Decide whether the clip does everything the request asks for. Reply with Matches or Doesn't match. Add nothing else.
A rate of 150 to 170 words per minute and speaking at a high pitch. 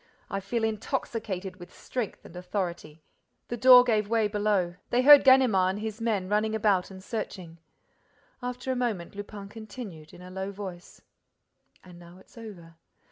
Matches